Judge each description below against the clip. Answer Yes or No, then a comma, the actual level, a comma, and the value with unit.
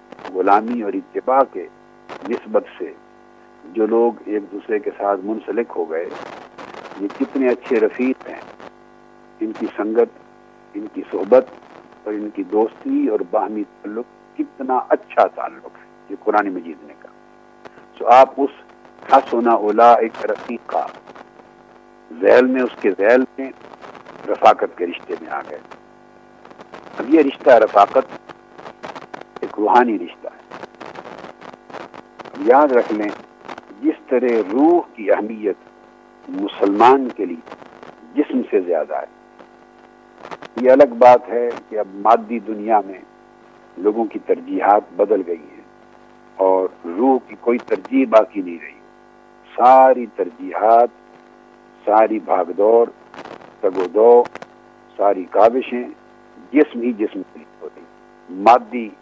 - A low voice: Yes, low, 130 Hz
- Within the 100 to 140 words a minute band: Yes, average, 125 wpm